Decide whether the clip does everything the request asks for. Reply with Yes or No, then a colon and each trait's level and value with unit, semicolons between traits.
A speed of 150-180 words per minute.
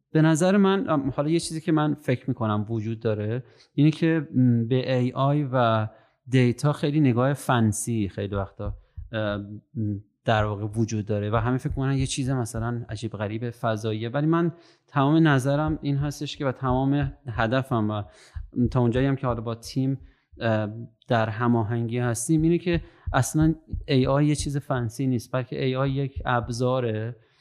Yes: fast, 155 wpm